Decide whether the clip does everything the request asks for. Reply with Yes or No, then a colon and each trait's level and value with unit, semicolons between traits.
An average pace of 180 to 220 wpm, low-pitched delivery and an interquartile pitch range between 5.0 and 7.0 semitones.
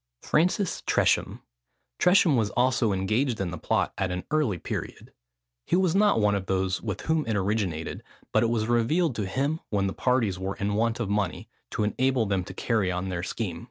Yes: average, 195 wpm; low, 110 Hz; average, 5.3 semitones